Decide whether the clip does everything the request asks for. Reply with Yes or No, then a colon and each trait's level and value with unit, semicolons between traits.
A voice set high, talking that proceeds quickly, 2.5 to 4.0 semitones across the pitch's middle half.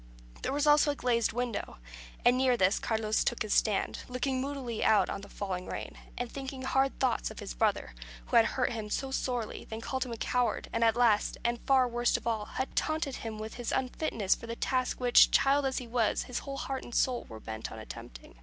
Yes: high, 240 Hz; fast, 220 wpm; average, 3.2 semitones